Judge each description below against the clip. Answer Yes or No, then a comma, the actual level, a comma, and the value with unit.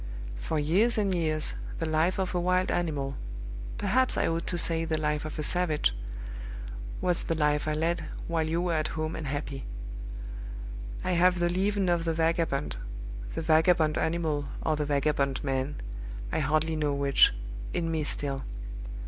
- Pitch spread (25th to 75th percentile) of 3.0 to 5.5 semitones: No, narrow, 2.5 semitones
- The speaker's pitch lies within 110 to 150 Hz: No, medium, 160 Hz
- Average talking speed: Yes, average, 165 wpm